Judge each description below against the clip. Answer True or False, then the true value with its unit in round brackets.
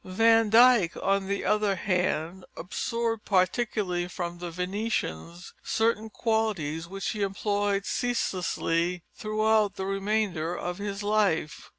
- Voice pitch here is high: True (195 Hz)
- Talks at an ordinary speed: False (115 wpm)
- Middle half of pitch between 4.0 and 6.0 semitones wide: False (3.3 semitones)